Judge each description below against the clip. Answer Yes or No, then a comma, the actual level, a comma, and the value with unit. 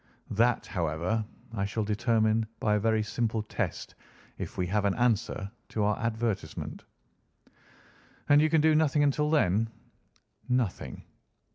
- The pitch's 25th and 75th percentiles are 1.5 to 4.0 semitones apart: Yes, average, 3.0 semitones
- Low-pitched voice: Yes, low, 110 Hz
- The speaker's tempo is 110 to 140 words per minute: Yes, slow, 135 wpm